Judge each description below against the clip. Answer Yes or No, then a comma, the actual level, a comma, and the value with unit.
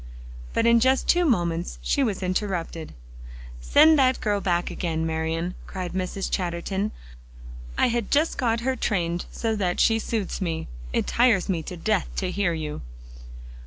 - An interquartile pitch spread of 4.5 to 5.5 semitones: Yes, average, 5.0 semitones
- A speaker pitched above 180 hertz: Yes, high, 190 Hz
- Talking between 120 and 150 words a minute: No, average, 160 wpm